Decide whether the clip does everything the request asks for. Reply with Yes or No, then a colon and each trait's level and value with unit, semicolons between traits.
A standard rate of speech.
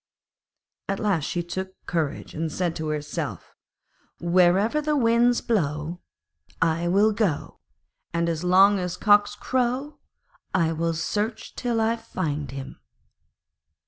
No: slow, 125 wpm